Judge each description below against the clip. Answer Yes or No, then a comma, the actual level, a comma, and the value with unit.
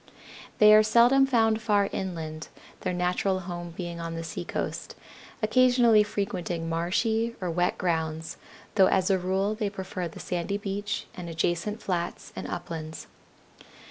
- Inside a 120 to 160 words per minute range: Yes, average, 140 wpm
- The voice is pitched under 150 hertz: No, medium, 185 Hz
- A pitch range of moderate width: Yes, average, 3.7 semitones